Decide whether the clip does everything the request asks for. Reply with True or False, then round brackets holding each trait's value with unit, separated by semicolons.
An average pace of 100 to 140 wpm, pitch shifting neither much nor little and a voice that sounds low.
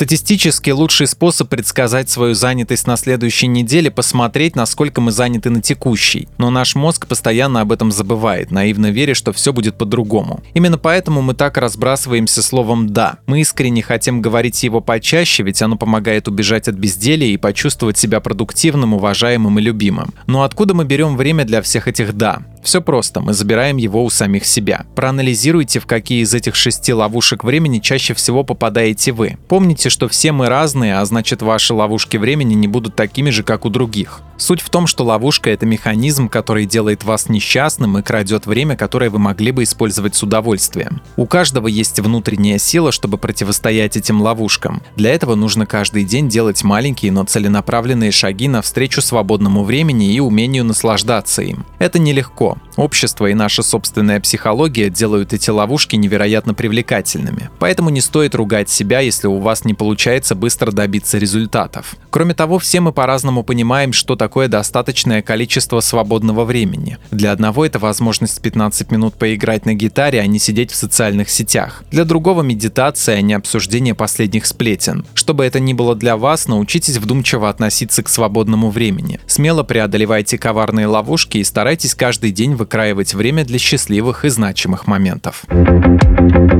False (160 wpm; 3.4 semitones; 115 Hz)